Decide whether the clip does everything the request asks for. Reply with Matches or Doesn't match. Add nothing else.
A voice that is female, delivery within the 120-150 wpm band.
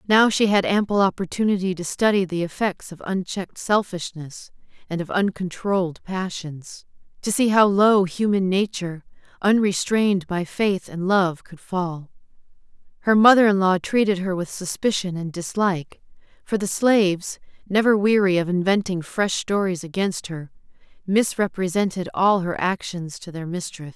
Matches